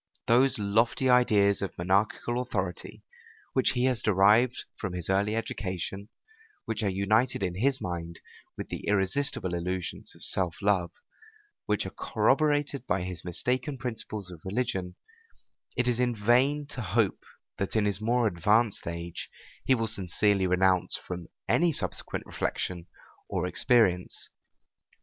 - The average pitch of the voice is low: Yes, low, 105 Hz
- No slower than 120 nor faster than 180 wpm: Yes, average, 140 wpm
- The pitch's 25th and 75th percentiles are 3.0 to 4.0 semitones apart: No, average, 4.9 semitones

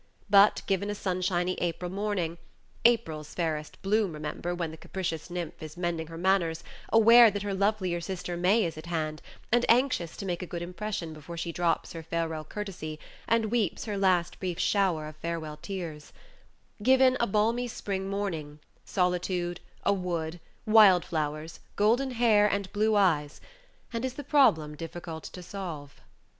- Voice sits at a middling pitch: Yes, medium, 180 Hz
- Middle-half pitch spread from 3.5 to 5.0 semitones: Yes, average, 4.0 semitones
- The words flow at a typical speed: Yes, average, 160 wpm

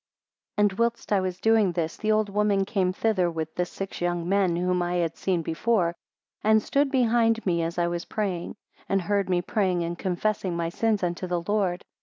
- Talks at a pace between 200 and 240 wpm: Yes, fast, 205 wpm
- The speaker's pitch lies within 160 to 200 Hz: Yes, medium, 185 Hz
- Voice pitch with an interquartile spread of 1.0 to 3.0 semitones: No, average, 3.4 semitones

